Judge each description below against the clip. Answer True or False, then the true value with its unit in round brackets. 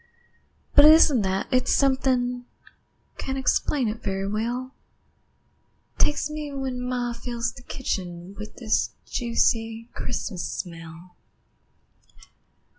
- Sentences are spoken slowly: True (110 wpm)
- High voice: True (240 Hz)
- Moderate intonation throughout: True (3.7 semitones)